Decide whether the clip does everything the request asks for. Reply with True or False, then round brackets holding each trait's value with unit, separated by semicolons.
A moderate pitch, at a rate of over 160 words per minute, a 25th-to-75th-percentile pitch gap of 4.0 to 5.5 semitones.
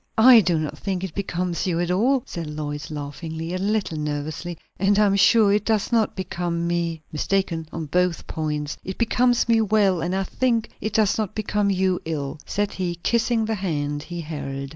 True (180 Hz; 195 wpm; 4.5 semitones)